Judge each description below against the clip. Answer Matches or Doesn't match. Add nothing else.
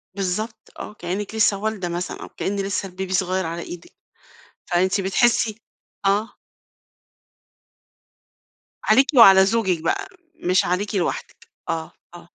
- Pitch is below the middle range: Doesn't match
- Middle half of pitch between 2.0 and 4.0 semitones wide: Matches